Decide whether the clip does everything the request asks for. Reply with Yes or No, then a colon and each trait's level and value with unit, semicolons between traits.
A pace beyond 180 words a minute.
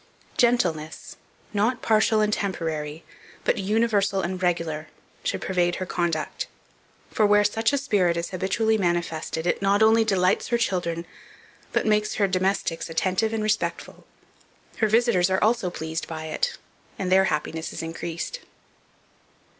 No: average, 140 wpm